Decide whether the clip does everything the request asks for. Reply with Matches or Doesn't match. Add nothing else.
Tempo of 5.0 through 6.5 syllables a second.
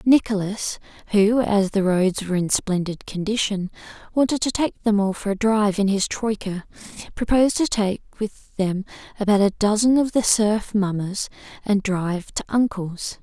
Doesn't match